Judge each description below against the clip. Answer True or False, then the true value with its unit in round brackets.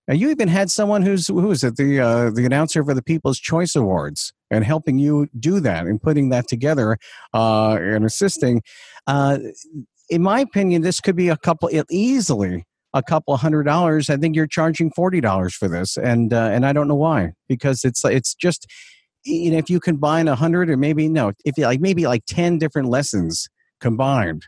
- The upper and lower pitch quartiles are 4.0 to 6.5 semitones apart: True (5.4 semitones)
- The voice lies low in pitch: False (145 Hz)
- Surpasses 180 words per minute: True (200 wpm)